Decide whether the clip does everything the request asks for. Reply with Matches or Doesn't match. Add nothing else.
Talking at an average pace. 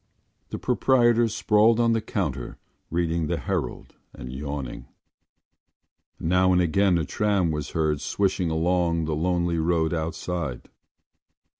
Doesn't match